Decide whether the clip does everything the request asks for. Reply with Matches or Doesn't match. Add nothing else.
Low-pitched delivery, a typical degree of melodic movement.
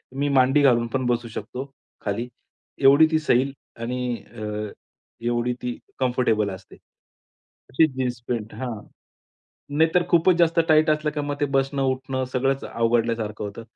Matches